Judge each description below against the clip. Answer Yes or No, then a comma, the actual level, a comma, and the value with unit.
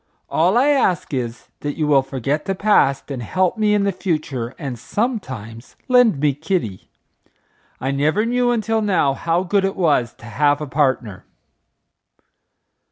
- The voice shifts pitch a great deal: Yes, wide, 7.0 semitones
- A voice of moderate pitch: Yes, medium, 155 Hz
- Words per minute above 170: No, average, 160 wpm